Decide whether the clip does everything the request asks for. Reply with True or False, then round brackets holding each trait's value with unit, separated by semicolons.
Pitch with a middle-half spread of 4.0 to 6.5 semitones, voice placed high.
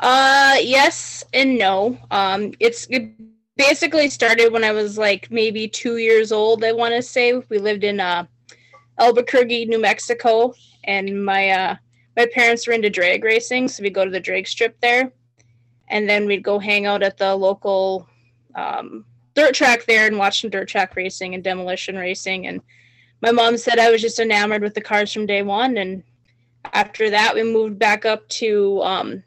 False (3.4 semitones; 210 Hz)